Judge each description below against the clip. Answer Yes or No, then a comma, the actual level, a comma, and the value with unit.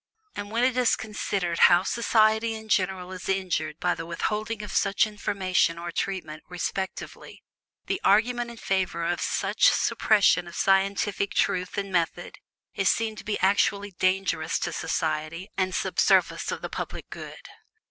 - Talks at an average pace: Yes, average, 155 wpm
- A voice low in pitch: No, high, 195 Hz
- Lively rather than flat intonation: No, average, 3.2 semitones